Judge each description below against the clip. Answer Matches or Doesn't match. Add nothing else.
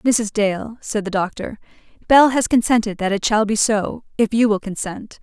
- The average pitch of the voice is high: Matches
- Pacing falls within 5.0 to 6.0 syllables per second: Doesn't match